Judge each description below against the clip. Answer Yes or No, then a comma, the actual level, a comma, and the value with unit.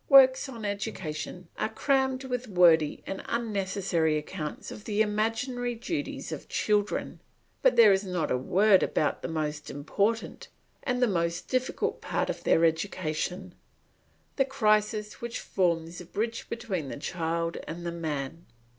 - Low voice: No, high, 195 Hz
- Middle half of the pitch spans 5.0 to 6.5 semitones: Yes, wide, 5.5 semitones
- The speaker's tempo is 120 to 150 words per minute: Yes, average, 145 wpm